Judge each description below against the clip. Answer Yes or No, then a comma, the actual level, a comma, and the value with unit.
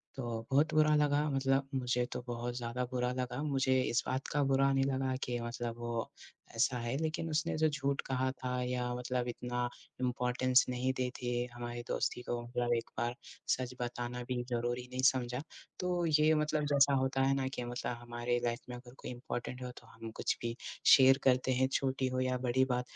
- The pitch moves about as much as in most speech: No, narrow, 1.6 semitones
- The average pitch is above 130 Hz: No, low, 125 Hz